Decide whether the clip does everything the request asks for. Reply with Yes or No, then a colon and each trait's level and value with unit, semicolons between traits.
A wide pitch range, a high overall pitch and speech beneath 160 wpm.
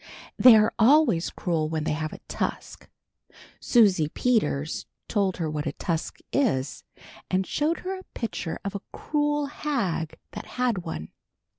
Yes: wide, 8.0 semitones; high, 195 Hz; average, 150 wpm